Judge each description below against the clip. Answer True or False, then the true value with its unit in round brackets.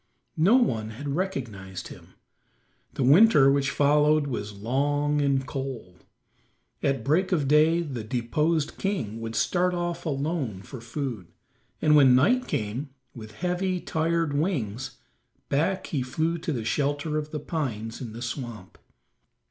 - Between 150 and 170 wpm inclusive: False (140 wpm)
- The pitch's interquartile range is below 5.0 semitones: False (5.3 semitones)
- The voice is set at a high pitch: False (140 Hz)